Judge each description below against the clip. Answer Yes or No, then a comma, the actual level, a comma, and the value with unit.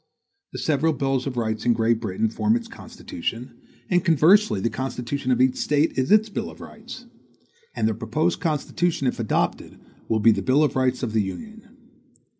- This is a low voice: Yes, low, 130 Hz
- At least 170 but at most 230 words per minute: Yes, average, 185 wpm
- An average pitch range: No, wide, 6.2 semitones